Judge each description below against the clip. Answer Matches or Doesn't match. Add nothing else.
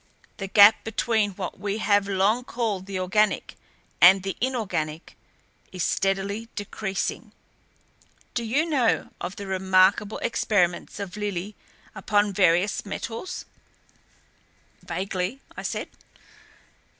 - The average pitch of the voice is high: Matches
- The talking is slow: Matches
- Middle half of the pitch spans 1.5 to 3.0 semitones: Matches